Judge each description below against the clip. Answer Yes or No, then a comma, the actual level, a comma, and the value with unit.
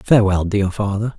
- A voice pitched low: Yes, low, 100 Hz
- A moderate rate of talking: Yes, average, 150 wpm